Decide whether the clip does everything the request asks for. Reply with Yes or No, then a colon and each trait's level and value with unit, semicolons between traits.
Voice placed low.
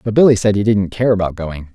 Yes: low, 100 Hz